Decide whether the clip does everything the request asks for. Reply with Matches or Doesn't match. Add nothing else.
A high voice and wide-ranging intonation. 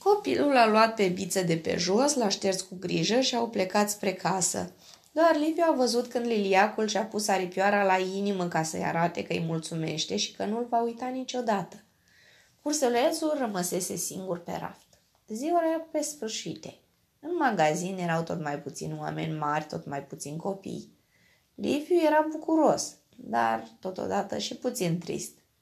Matches